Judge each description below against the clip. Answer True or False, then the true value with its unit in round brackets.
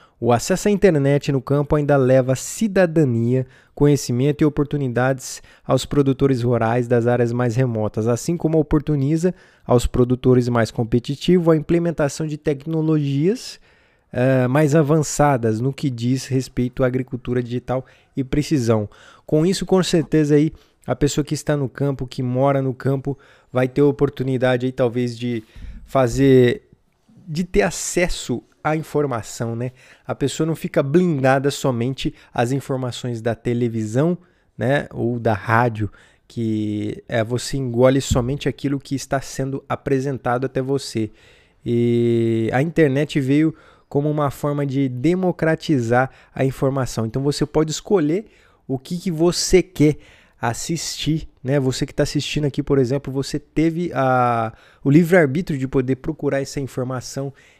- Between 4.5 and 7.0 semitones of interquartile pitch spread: False (3.5 semitones)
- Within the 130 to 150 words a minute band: True (145 wpm)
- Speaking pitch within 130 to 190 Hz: True (135 Hz)